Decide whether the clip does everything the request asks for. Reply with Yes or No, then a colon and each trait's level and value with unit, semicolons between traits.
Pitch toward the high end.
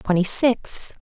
Yes: high, 210 Hz